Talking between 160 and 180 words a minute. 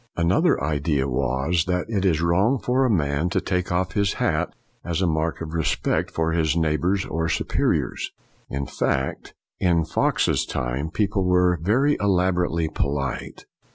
No: average, 150 wpm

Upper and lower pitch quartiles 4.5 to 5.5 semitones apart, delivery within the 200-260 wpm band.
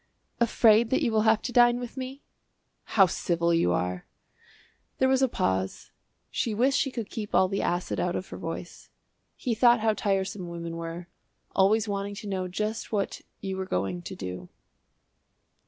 No: average, 4.9 semitones; average, 175 wpm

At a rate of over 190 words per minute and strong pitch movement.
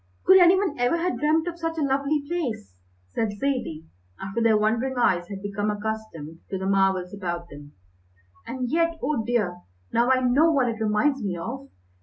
No: average, 185 wpm; wide, 6.4 semitones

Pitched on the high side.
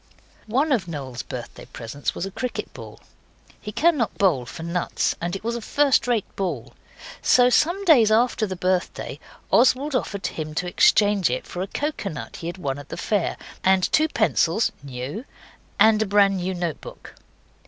Yes: high, 195 Hz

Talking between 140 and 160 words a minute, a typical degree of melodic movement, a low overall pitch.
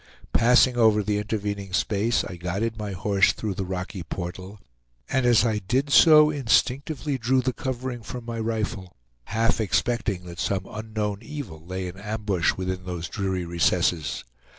Yes: average, 155 wpm; average, 4.2 semitones; low, 105 Hz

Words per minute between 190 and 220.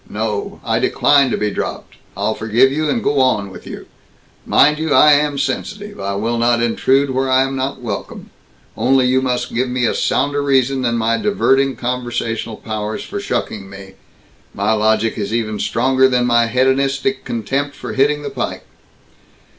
No: average, 175 wpm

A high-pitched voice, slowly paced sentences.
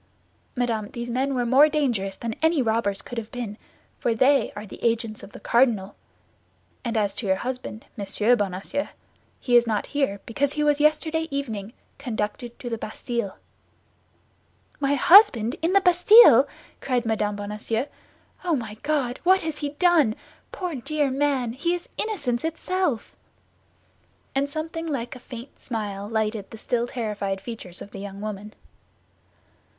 No: high, 240 Hz; average, 155 wpm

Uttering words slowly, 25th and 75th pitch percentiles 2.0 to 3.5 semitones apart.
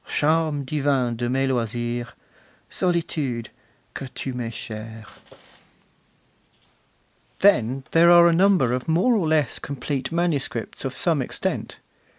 No: slow, 120 wpm; average, 5.2 semitones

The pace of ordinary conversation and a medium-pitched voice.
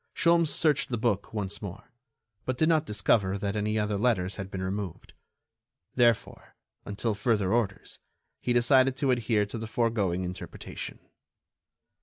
No: average, 145 wpm; low, 110 Hz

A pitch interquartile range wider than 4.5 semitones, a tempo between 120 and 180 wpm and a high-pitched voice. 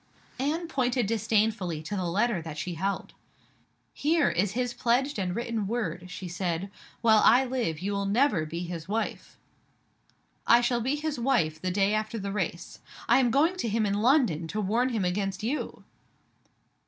Yes: average, 5.0 semitones; average, 175 wpm; high, 210 Hz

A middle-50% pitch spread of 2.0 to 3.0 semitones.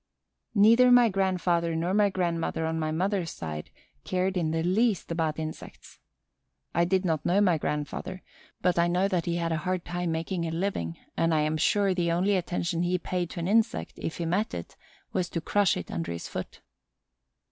Yes: average, 2.7 semitones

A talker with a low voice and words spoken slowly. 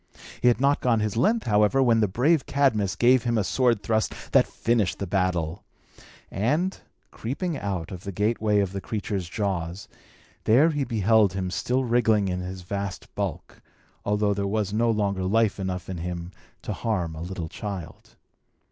No: low, 105 Hz; average, 170 wpm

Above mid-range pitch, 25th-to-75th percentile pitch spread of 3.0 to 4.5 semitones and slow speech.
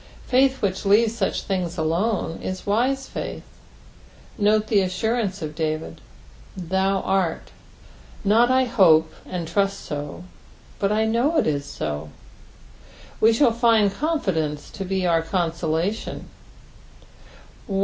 No: high, 195 Hz; average, 5.3 semitones; slow, 125 wpm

